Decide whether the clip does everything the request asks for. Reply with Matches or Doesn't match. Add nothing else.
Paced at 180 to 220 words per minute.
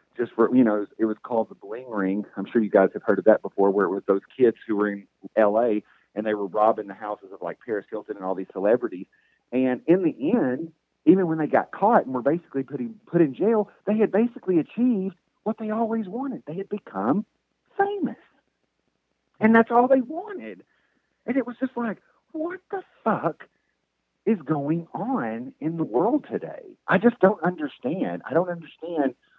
Matches